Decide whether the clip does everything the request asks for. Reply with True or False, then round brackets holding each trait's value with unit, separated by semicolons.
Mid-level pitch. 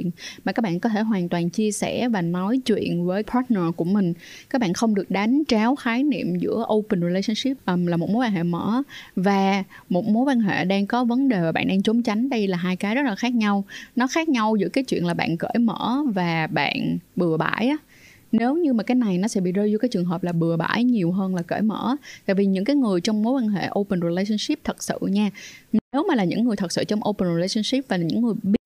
False (210 Hz)